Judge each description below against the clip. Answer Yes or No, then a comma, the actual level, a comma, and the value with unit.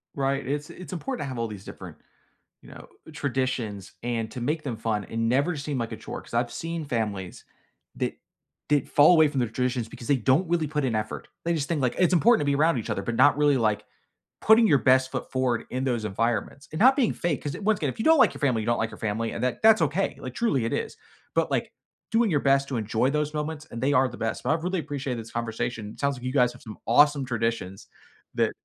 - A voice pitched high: No, low, 130 Hz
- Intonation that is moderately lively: Yes, average, 4.6 semitones